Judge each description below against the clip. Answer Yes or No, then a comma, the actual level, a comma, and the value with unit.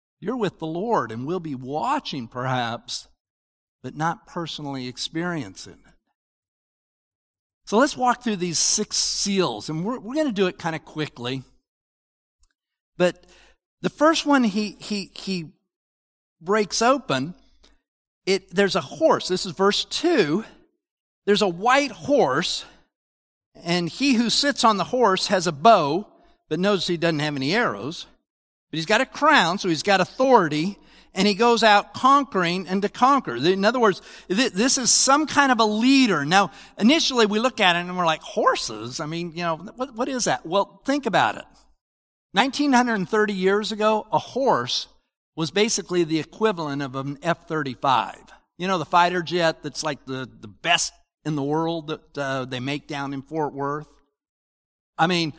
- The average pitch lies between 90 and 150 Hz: No, medium, 180 Hz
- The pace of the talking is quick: No, average, 170 wpm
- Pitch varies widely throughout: Yes, wide, 6.5 semitones